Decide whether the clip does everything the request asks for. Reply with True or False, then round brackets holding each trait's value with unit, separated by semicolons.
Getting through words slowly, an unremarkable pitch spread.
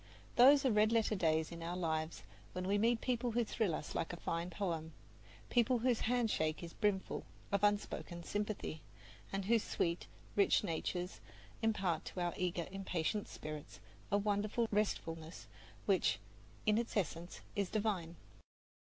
False (150 wpm; 4.4 semitones)